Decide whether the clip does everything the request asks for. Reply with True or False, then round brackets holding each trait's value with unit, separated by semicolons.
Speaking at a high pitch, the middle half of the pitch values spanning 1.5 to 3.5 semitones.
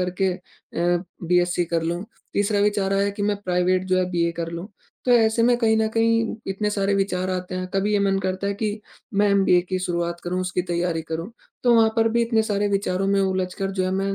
True (195 Hz; 2.4 semitones)